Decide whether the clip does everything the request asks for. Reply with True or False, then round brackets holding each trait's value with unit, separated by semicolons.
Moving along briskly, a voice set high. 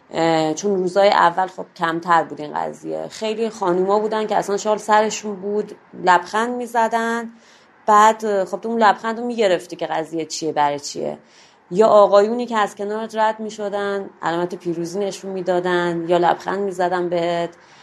True (170 wpm; 195 Hz)